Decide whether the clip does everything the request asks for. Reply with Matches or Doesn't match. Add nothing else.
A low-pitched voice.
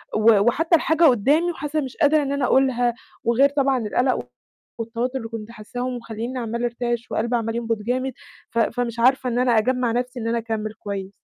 Doesn't match